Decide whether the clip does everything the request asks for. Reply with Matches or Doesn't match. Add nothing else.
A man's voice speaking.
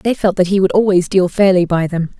Doesn't match